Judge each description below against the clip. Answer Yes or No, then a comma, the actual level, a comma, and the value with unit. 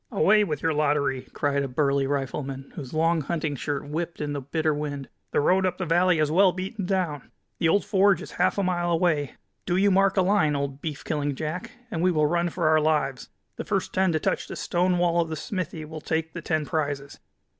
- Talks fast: Yes, fast, 225 wpm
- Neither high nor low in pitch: Yes, medium, 160 Hz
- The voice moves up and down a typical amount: Yes, average, 3.7 semitones